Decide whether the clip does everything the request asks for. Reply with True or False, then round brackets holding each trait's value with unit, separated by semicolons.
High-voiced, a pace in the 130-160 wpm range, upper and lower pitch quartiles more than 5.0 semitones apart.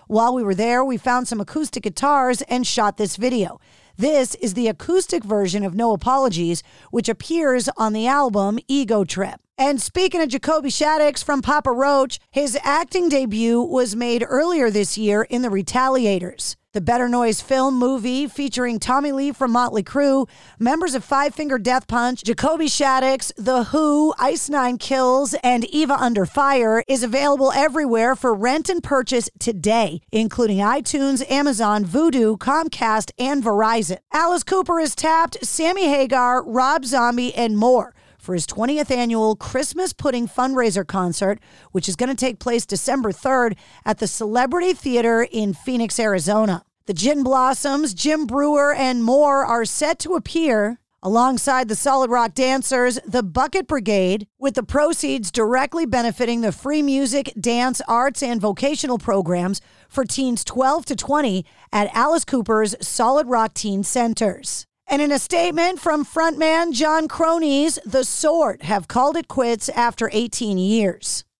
False (255 Hz; 155 wpm; 4.1 semitones)